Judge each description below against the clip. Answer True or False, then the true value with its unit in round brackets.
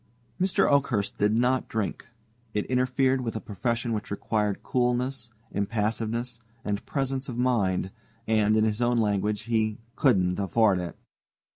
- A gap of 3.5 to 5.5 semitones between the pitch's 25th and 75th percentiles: False (3.1 semitones)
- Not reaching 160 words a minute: True (140 wpm)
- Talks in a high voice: False (115 Hz)